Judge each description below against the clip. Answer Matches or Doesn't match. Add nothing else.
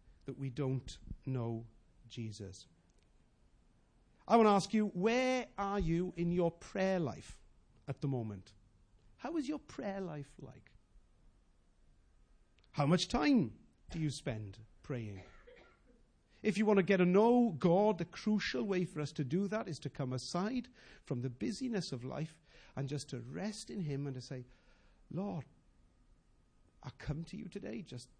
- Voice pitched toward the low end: Doesn't match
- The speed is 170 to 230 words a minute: Doesn't match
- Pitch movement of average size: Doesn't match